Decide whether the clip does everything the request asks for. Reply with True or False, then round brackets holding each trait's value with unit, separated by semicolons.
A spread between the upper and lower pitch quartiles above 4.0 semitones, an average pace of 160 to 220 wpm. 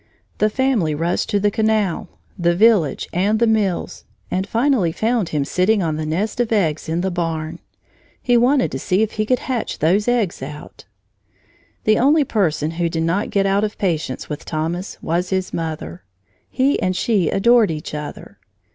True (5.1 semitones; 180 wpm)